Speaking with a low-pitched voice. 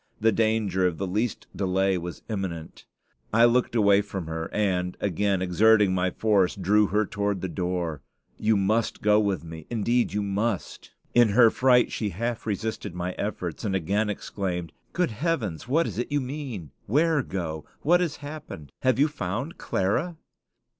Yes: low, 105 Hz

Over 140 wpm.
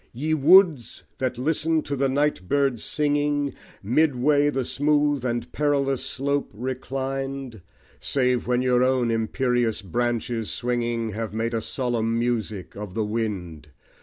No: slow, 135 wpm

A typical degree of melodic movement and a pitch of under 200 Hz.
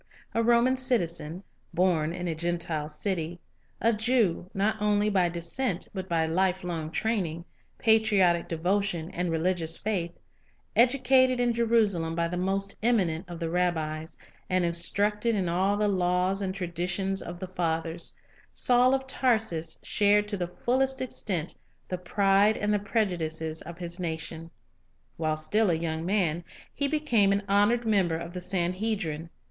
Yes: average, 3.9 semitones; medium, 185 Hz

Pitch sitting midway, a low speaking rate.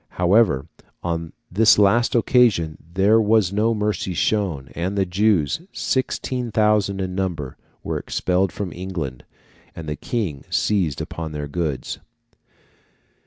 No: very low, 95 Hz; slow, 125 wpm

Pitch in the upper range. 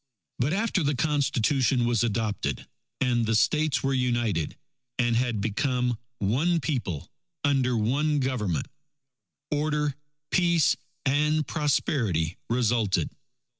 No: low, 125 Hz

